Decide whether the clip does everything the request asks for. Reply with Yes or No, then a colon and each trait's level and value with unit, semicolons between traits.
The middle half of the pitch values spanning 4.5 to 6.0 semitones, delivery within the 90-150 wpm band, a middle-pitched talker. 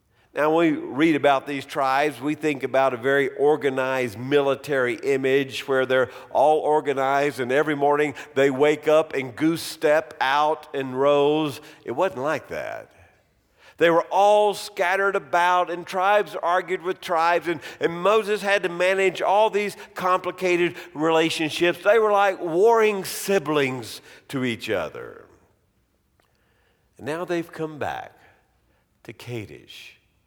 Yes: average, 4.8 semitones; average, 140 wpm; medium, 155 Hz